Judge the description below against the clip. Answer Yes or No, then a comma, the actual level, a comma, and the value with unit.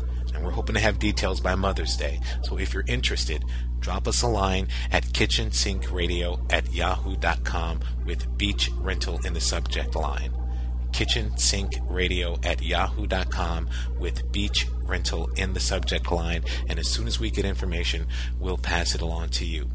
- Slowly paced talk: No, average, 160 wpm